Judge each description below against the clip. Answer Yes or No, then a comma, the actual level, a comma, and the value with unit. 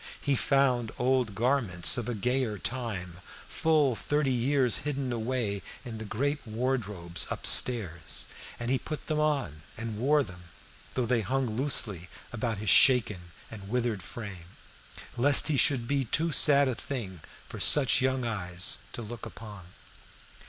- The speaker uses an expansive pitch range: No, average, 4.3 semitones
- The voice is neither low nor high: No, low, 120 Hz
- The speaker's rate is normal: Yes, average, 150 wpm